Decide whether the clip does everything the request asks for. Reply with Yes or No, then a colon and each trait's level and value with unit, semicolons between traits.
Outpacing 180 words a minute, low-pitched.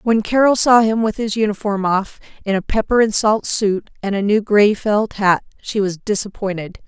No: average, 200 wpm; high, 210 Hz